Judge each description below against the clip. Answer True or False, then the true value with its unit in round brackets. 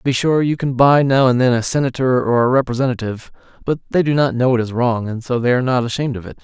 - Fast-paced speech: True (280 wpm)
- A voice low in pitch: True (125 Hz)